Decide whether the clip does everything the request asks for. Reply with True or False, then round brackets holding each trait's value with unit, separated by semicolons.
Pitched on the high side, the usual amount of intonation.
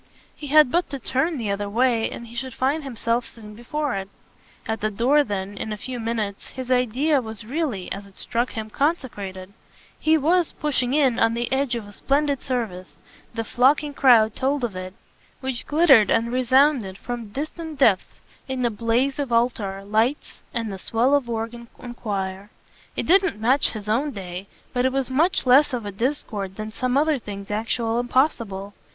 True (240 Hz; 4.3 semitones)